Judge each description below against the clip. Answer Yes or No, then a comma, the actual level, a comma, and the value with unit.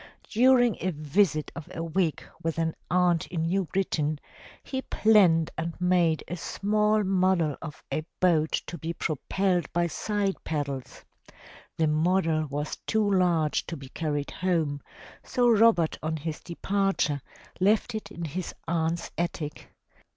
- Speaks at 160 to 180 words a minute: No, average, 145 wpm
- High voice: No, medium, 170 Hz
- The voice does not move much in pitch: No, average, 3.6 semitones